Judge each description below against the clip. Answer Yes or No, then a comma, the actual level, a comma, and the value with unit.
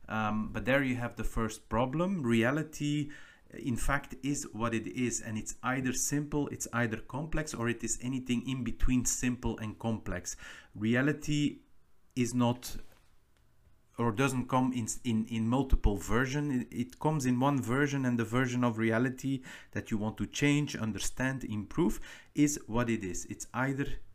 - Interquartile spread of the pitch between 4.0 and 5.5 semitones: No, average, 3.3 semitones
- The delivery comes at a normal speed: Yes, average, 160 wpm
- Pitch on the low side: Yes, low, 120 Hz